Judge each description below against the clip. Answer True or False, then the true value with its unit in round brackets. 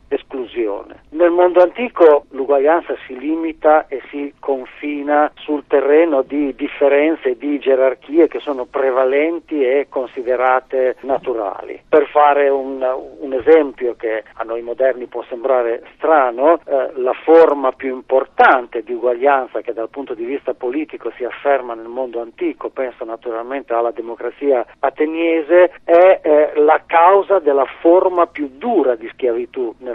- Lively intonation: False (4.4 semitones)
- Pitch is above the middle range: False (140 Hz)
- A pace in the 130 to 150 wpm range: True (140 wpm)